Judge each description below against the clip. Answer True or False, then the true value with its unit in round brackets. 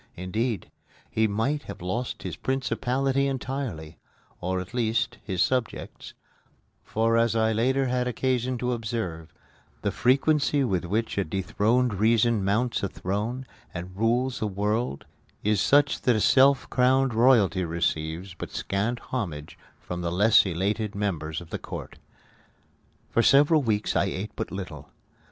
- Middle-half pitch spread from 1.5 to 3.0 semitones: False (5.1 semitones)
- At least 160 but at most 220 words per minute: False (140 wpm)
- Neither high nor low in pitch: False (110 Hz)